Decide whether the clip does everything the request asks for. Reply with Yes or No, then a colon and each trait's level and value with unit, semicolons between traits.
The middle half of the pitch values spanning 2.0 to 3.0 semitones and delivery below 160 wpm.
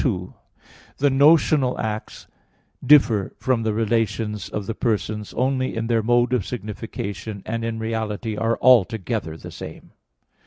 Yes: narrow, 2.6 semitones; average, 140 wpm